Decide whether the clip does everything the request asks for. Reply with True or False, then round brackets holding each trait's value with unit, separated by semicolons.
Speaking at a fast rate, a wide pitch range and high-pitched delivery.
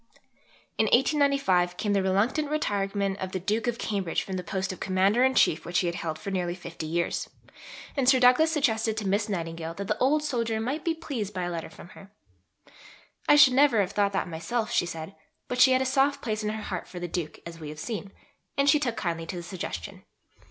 True (225 wpm; 6.1 semitones; 200 Hz)